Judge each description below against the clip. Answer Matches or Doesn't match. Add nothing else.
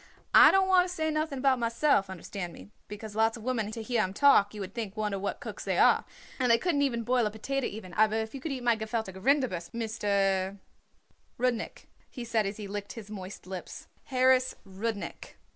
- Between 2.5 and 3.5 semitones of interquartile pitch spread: Doesn't match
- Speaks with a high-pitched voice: Matches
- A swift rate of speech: Matches